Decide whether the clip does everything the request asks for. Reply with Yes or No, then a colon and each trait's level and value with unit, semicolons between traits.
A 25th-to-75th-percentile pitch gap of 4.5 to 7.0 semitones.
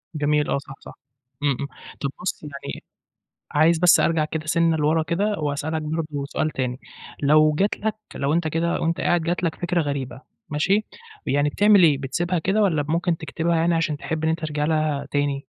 No: narrow, 2.5 semitones